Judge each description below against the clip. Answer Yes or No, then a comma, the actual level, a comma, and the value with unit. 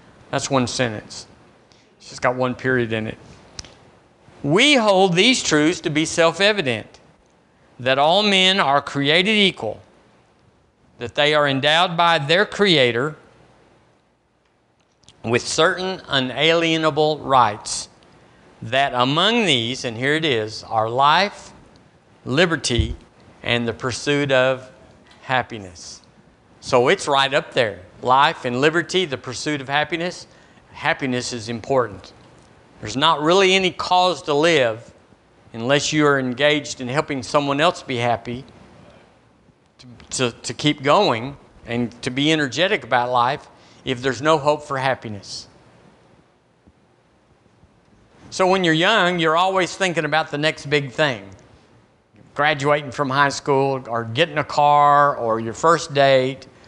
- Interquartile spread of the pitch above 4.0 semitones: Yes, average, 4.4 semitones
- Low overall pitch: No, medium, 145 Hz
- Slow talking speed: Yes, slow, 130 wpm